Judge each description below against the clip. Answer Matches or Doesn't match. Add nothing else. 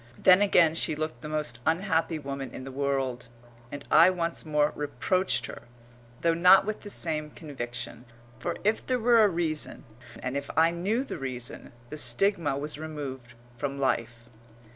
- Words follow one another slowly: Doesn't match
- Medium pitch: Matches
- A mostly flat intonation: Doesn't match